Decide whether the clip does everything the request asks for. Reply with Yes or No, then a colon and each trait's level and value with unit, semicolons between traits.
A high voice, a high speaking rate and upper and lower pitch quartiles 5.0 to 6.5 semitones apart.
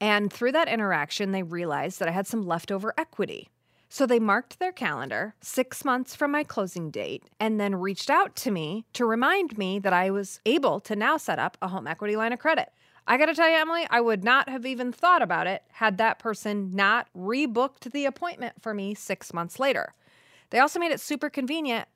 Yes: high, 225 Hz; fast, 210 wpm; wide, 5.6 semitones